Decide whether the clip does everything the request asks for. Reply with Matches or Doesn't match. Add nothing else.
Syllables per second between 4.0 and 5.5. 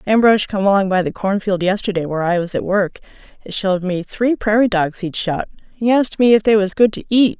Doesn't match